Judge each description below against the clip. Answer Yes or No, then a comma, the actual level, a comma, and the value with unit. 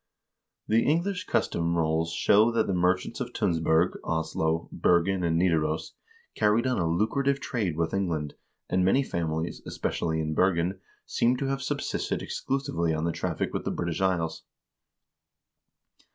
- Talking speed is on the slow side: No, average, 150 wpm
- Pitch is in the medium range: No, very low, 90 Hz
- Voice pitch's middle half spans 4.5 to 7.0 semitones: Yes, average, 5.3 semitones